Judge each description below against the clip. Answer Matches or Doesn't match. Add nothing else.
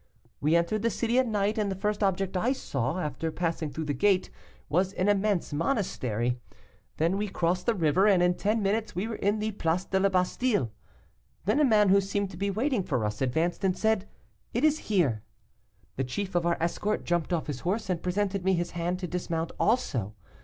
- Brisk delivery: Matches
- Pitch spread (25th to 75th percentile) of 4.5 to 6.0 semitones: Doesn't match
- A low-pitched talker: Doesn't match